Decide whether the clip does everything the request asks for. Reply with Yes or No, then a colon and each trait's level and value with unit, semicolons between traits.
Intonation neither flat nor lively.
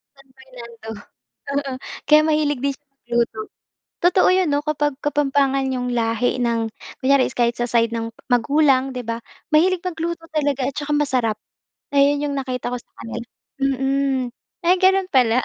Yes: average, 3.3 semitones